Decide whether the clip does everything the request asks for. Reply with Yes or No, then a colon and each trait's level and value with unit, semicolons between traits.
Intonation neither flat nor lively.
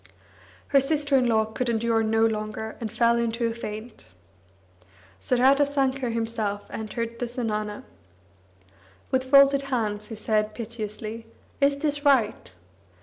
Yes: average, 3.2 semitones